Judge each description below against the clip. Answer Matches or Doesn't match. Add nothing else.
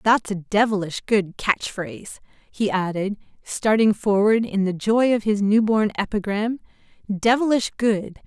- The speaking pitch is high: Matches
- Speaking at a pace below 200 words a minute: Matches